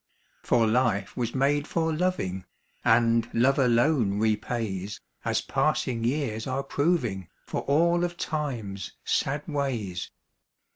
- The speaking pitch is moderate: No, low, 120 Hz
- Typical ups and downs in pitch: Yes, average, 5.0 semitones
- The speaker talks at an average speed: No, slow, 115 wpm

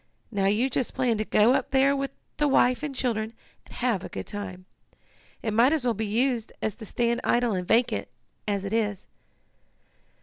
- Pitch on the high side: Yes, high, 230 Hz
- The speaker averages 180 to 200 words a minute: Yes, average, 195 wpm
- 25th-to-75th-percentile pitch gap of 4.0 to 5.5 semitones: No, average, 3.4 semitones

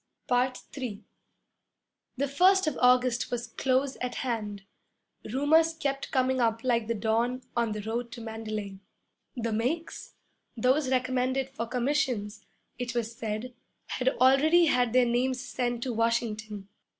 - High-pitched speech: Yes, high, 245 Hz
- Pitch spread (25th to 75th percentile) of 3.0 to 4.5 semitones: No, narrow, 2.4 semitones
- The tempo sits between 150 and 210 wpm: No, slow, 135 wpm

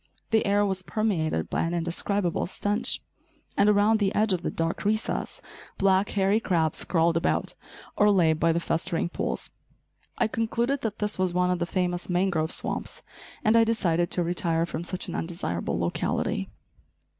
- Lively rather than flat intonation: No, average, 3.6 semitones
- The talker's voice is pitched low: No, medium, 185 Hz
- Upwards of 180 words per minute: No, average, 165 wpm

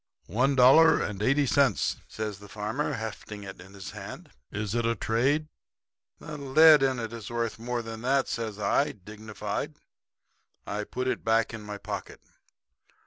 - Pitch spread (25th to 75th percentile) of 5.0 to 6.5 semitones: No, average, 4.0 semitones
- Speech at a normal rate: Yes, average, 165 wpm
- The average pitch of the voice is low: Yes, low, 115 Hz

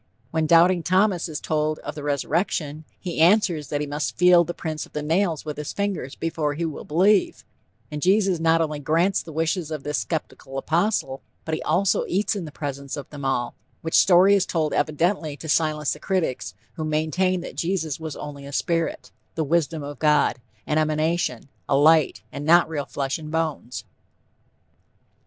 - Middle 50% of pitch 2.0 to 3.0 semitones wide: Yes, average, 2.7 semitones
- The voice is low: No, medium, 160 Hz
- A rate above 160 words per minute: Yes, average, 185 wpm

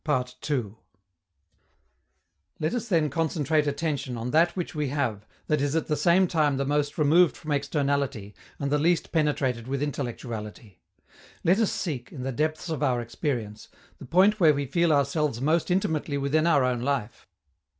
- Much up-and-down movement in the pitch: No, average, 3.4 semitones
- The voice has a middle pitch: Yes, medium, 145 Hz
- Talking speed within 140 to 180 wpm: Yes, average, 160 wpm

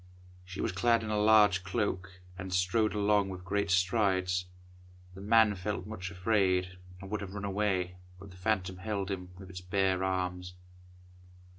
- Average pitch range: No, narrow, 2.2 semitones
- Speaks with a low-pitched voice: Yes, very low, 95 Hz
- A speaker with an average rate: Yes, average, 165 wpm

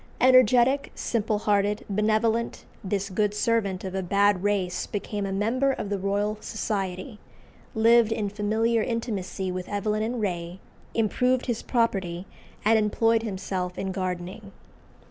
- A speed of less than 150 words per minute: Yes, slow, 135 wpm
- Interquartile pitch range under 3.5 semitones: Yes, average, 2.8 semitones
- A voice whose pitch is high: Yes, high, 210 Hz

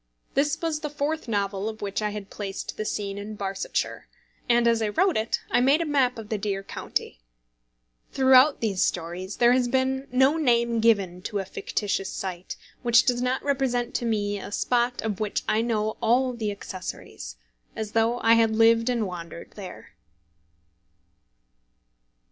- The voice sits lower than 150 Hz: No, high, 225 Hz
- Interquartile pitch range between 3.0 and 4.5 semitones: Yes, average, 3.7 semitones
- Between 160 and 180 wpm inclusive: Yes, average, 170 wpm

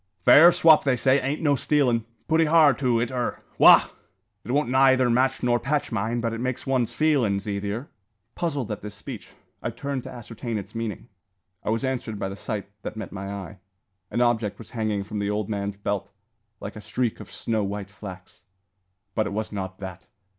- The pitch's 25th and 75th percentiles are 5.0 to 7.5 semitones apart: No, average, 4.2 semitones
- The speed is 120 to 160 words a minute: No, average, 195 wpm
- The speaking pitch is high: No, low, 115 Hz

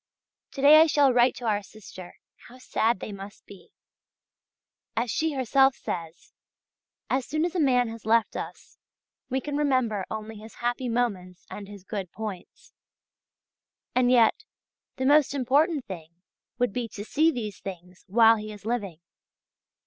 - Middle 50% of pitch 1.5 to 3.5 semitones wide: No, average, 4.4 semitones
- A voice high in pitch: Yes, high, 230 Hz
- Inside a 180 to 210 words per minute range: No, average, 155 wpm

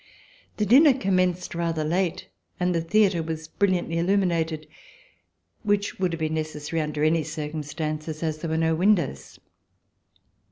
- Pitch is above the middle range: No, medium, 165 Hz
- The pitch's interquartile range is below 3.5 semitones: Yes, average, 2.8 semitones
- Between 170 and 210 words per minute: No, slow, 135 wpm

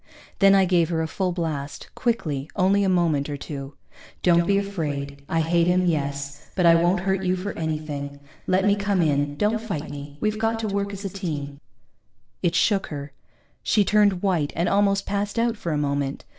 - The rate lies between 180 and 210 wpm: Yes, average, 200 wpm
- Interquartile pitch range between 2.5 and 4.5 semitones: No, average, 5.3 semitones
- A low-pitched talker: No, medium, 175 Hz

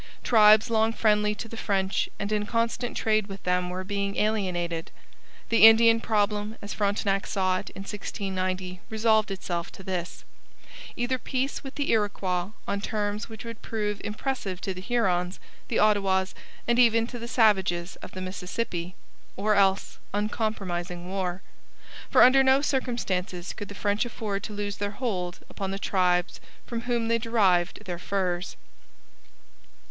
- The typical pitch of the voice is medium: No, high, 205 Hz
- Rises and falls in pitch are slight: No, average, 3.2 semitones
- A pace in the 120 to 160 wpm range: Yes, average, 155 wpm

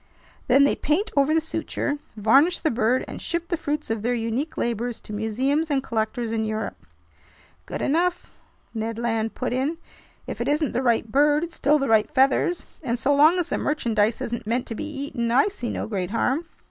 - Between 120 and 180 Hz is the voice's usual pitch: No, very high, 260 Hz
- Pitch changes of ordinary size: Yes, average, 4.9 semitones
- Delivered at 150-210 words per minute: Yes, average, 200 wpm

